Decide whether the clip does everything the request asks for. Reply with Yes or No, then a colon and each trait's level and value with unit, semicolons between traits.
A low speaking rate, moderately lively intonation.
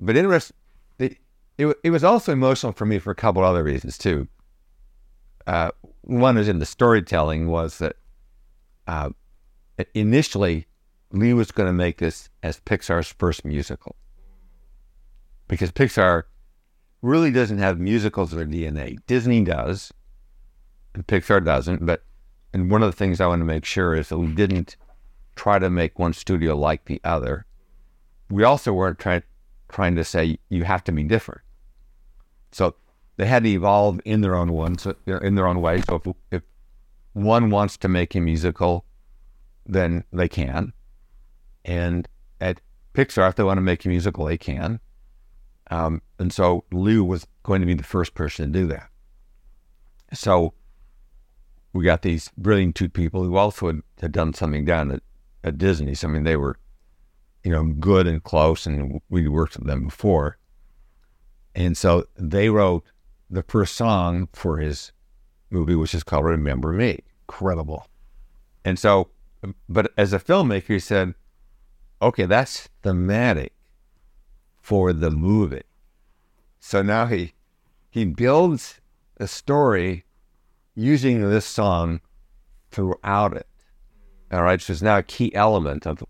No: average, 155 wpm; average, 3.8 semitones